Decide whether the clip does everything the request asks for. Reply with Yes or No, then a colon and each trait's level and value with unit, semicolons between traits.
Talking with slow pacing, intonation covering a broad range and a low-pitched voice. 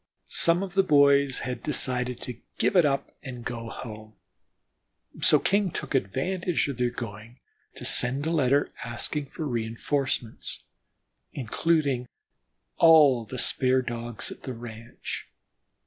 No: slow, 130 wpm; average, 3.9 semitones; low, 130 Hz